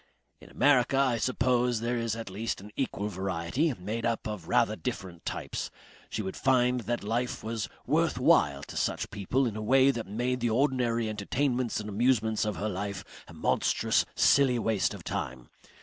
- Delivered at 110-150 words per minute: No, average, 180 wpm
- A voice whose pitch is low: Yes, low, 115 Hz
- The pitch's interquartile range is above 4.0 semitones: No, average, 3.4 semitones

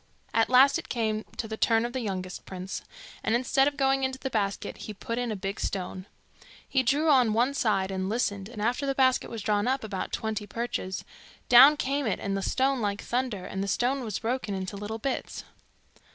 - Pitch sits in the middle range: No, high, 225 Hz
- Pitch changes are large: No, average, 4.3 semitones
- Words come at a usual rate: No, fast, 210 wpm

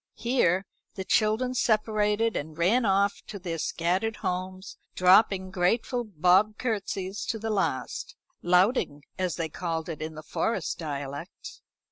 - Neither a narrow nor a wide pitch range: Yes, average, 4.1 semitones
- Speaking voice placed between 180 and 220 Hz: Yes, high, 190 Hz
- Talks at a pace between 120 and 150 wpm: Yes, slow, 135 wpm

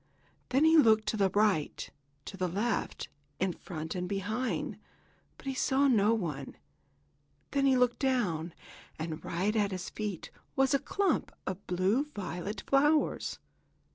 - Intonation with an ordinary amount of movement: No, wide, 6.3 semitones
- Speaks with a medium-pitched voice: No, high, 210 Hz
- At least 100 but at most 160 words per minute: Yes, average, 145 wpm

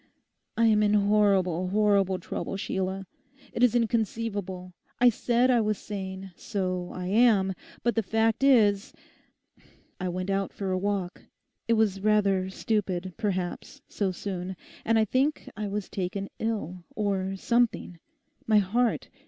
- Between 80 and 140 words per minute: Yes, slow, 135 wpm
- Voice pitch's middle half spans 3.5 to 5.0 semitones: No, average, 2.9 semitones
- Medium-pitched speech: No, high, 200 Hz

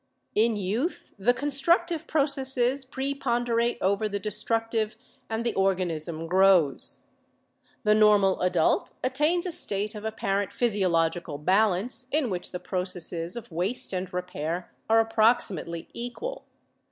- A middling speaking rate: No, slow, 120 wpm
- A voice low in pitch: No, high, 210 Hz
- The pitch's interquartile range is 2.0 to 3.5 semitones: No, average, 5.1 semitones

